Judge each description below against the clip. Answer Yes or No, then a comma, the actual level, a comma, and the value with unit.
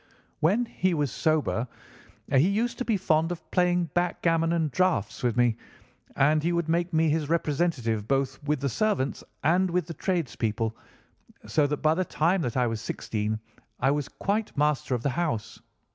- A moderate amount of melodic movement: Yes, average, 4.9 semitones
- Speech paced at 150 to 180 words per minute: Yes, average, 175 wpm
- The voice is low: No, medium, 155 Hz